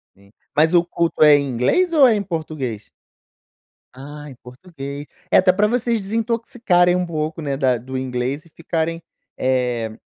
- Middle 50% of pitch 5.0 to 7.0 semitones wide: Yes, wide, 5.6 semitones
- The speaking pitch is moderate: Yes, medium, 155 Hz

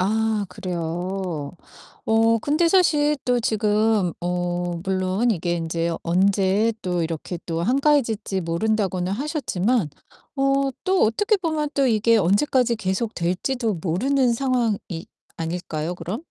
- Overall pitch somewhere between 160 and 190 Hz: No, high, 210 Hz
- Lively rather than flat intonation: Yes, wide, 5.8 semitones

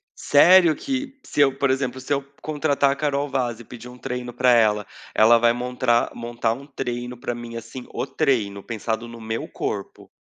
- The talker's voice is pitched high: No, low, 125 Hz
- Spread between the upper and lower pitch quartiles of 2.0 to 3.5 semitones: Yes, average, 2.9 semitones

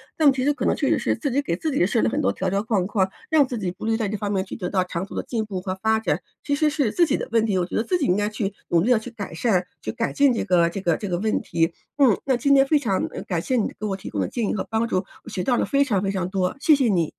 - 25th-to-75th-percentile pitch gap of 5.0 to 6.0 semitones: Yes, average, 5.3 semitones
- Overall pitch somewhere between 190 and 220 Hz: Yes, high, 215 Hz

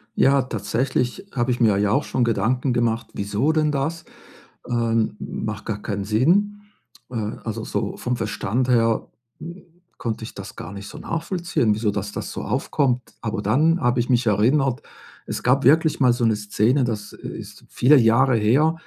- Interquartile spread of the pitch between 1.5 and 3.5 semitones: No, average, 4.1 semitones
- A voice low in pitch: Yes, low, 120 Hz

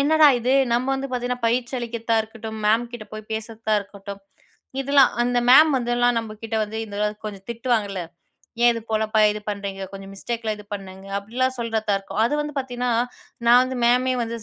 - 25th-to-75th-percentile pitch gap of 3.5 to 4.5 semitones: No, average, 2.7 semitones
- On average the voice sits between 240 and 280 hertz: No, high, 230 Hz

